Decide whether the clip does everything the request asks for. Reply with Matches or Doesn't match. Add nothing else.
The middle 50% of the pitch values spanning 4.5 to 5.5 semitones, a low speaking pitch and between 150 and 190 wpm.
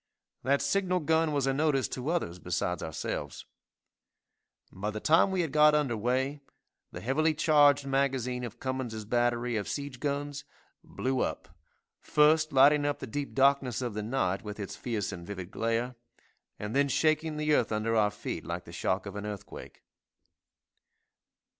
Matches